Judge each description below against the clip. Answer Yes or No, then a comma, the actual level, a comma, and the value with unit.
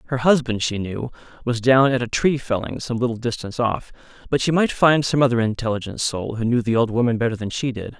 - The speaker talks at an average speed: No, fast, 235 wpm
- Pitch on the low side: Yes, low, 120 Hz